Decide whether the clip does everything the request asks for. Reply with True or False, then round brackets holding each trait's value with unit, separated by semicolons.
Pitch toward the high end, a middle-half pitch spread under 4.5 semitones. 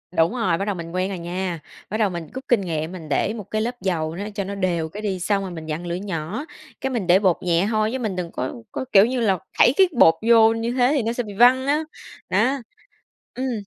False (200 Hz; 5.0 semitones)